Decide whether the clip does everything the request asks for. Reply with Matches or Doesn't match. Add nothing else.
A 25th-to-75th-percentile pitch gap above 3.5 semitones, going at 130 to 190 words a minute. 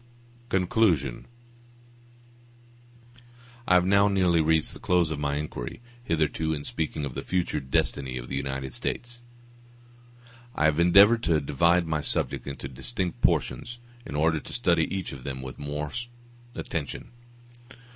Matches